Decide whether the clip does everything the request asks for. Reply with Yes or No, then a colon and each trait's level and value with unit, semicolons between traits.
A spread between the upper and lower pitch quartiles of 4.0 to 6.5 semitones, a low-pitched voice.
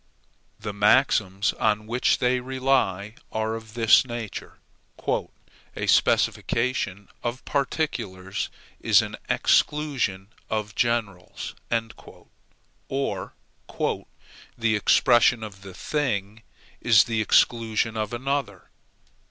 No: average, 3.6 semitones; low, 110 Hz